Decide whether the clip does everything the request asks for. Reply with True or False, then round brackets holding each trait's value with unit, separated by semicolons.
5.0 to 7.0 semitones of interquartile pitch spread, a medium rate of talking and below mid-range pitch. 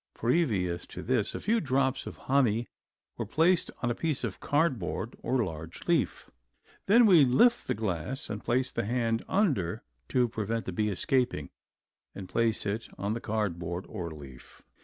True (5.3 semitones; 170 wpm; 115 Hz)